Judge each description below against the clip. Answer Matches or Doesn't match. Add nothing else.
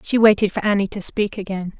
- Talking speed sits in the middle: Doesn't match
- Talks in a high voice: Matches